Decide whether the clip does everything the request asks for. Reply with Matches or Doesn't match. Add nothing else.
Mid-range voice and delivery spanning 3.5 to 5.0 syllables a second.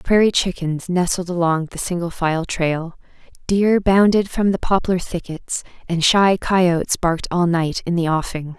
Matches